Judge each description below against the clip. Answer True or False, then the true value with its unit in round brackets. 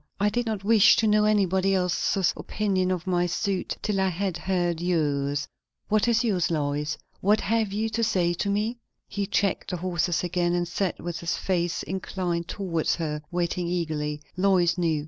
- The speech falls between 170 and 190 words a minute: True (180 wpm)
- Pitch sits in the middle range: True (180 Hz)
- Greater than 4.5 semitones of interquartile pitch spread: False (2.8 semitones)